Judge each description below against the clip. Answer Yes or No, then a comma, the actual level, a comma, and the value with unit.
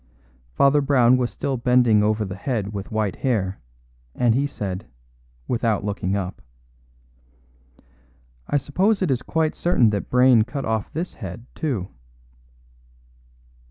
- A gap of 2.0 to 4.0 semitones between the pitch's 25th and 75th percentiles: No, average, 4.8 semitones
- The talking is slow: Yes, slow, 130 wpm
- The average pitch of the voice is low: Yes, low, 120 Hz